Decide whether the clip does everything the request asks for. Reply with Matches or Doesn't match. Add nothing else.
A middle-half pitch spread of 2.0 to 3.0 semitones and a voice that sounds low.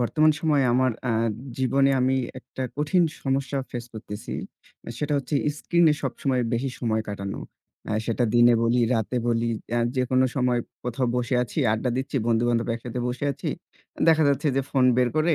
Matches